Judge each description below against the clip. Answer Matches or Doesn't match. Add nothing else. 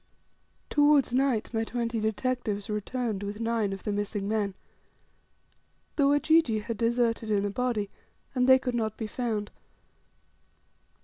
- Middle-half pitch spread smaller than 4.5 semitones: Matches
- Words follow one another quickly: Doesn't match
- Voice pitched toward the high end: Matches